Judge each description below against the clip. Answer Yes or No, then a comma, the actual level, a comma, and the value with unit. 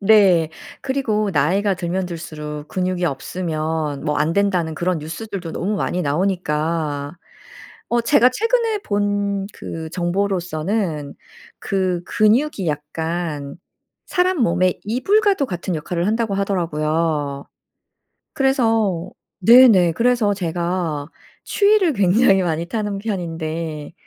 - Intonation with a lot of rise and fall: No, average, 4.8 semitones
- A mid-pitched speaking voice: Yes, medium, 180 Hz